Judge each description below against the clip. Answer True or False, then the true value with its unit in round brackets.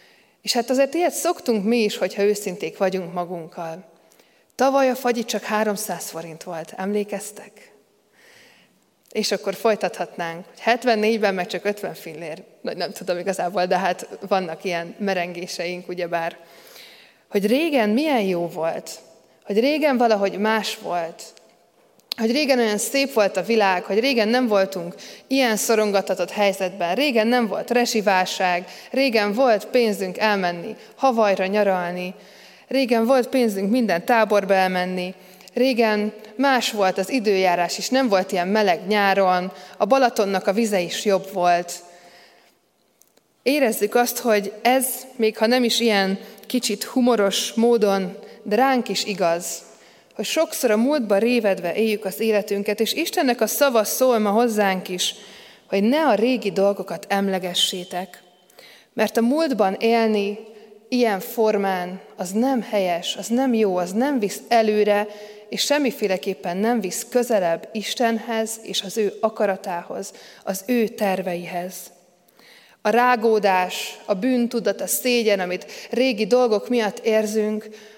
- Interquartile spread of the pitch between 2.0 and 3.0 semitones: False (3.9 semitones)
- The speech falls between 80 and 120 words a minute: False (135 wpm)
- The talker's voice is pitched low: False (210 Hz)